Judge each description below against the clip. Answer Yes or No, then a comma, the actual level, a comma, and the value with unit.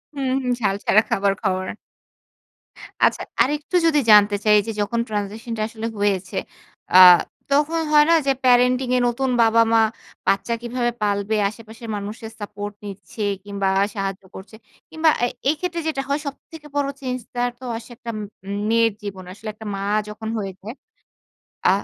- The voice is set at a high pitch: Yes, high, 225 Hz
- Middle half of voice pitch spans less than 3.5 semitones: No, average, 3.8 semitones